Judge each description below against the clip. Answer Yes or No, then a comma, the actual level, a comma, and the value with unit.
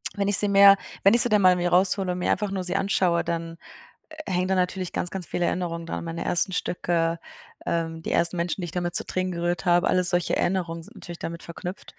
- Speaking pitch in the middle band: Yes, medium, 180 Hz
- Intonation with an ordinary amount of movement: No, narrow, 2.0 semitones